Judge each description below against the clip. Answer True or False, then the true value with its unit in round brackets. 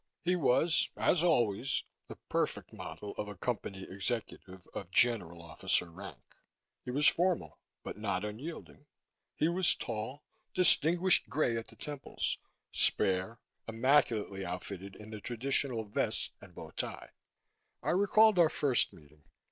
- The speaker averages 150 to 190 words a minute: False (135 wpm)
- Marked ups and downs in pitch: True (7.3 semitones)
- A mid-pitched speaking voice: False (115 Hz)